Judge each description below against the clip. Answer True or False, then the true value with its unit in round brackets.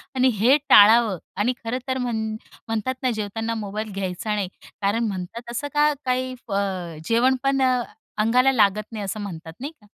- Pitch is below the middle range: False (225 Hz)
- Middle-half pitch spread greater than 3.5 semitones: True (4.0 semitones)